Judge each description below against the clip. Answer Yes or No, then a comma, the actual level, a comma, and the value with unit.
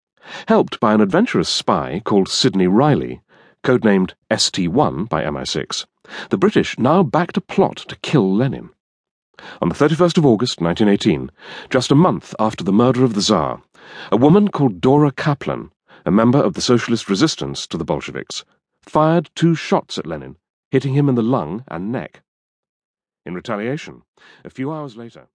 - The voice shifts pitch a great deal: Yes, wide, 5.9 semitones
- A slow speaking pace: No, average, 160 wpm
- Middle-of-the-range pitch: No, low, 130 Hz